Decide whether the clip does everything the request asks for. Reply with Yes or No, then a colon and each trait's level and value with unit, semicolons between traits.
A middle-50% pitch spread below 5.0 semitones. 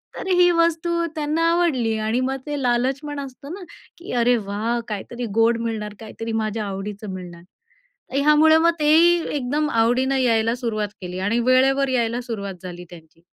No: wide, 5.5 semitones